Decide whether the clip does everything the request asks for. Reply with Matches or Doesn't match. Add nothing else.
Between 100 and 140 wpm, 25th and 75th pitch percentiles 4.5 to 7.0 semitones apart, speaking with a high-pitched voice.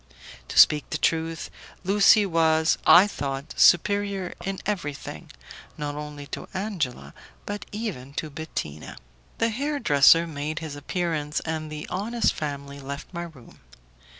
Doesn't match